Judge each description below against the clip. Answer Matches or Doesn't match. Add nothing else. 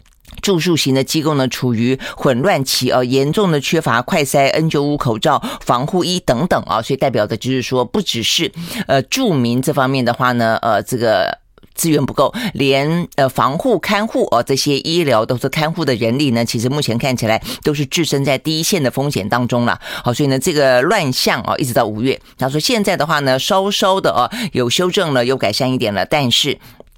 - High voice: Doesn't match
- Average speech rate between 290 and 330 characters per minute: Matches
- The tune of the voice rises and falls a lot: Doesn't match